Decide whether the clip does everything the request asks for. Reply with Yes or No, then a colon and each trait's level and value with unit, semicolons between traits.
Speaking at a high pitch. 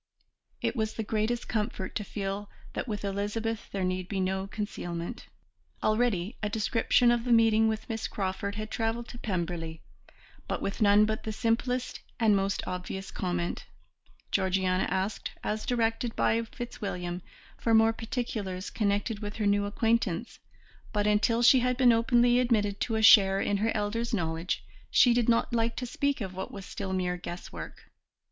Yes: high, 210 Hz